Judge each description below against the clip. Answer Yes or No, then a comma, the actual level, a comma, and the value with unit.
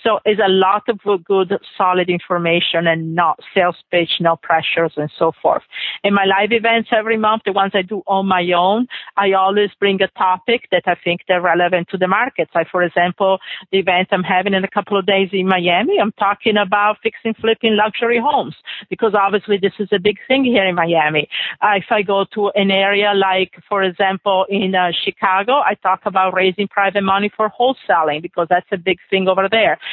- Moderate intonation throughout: No, narrow, 2.3 semitones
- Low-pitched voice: No, high, 195 Hz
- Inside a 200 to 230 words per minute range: Yes, fast, 205 wpm